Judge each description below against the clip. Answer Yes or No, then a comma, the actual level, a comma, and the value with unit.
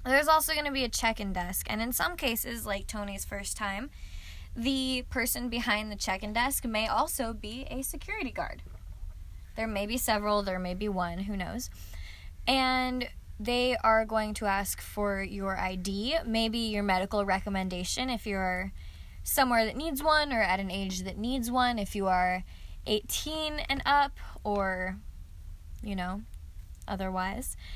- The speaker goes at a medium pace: Yes, average, 165 wpm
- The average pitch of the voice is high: Yes, high, 205 Hz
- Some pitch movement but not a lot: Yes, average, 4.9 semitones